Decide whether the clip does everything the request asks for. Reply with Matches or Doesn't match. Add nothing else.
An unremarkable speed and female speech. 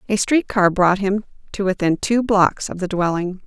Doesn't match